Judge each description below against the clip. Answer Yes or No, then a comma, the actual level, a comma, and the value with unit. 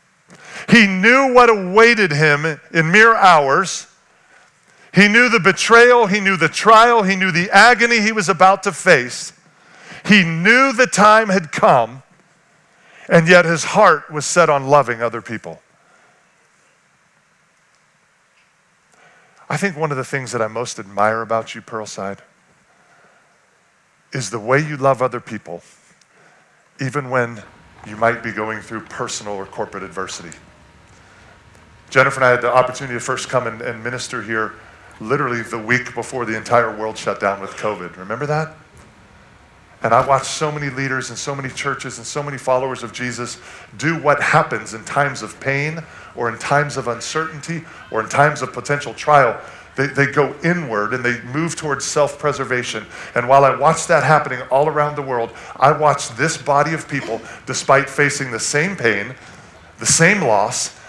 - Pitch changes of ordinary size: No, wide, 5.8 semitones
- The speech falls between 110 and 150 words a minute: No, average, 165 wpm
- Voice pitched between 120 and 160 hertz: Yes, low, 135 Hz